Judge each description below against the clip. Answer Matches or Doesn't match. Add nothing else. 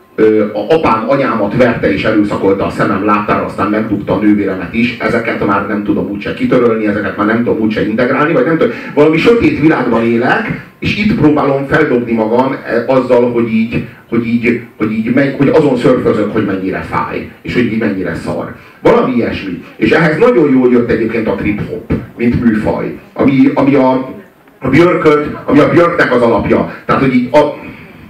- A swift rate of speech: Matches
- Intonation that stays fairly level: Doesn't match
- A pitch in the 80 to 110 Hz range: Doesn't match